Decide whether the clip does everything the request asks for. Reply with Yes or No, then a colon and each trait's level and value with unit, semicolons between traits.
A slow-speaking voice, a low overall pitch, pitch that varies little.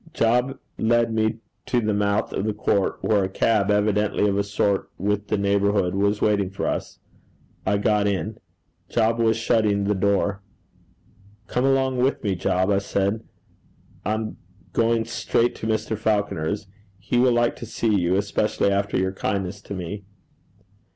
No: average, 160 wpm; low, 105 Hz; narrow, 2.0 semitones